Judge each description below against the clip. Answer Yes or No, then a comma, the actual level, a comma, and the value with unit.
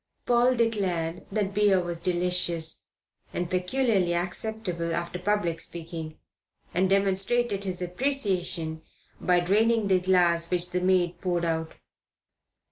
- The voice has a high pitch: No, medium, 180 Hz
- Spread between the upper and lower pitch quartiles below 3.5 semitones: Yes, average, 2.7 semitones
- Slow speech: Yes, slow, 120 wpm